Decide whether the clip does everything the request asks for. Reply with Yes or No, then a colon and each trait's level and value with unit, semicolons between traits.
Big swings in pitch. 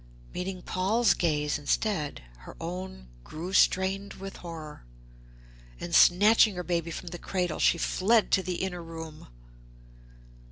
No: average, 2.7 semitones